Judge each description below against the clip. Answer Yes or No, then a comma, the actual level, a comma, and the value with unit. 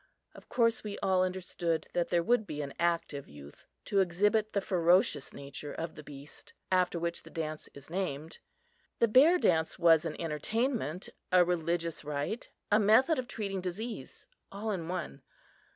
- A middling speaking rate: Yes, average, 165 wpm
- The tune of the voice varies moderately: Yes, average, 4.4 semitones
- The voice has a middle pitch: Yes, medium, 175 Hz